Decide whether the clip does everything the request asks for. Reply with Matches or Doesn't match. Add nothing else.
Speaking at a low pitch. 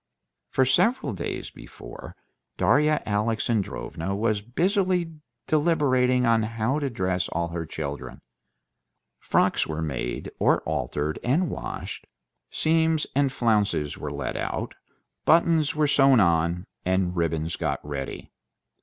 Matches